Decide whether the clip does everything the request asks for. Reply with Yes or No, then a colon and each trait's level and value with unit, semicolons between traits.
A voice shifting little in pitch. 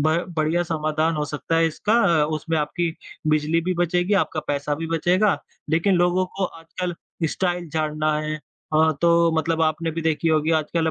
Yes: narrow, 2.0 semitones